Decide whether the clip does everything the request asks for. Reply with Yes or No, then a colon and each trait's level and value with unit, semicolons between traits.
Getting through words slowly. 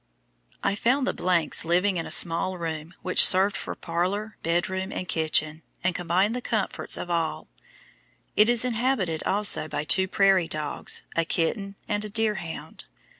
No: average, 160 wpm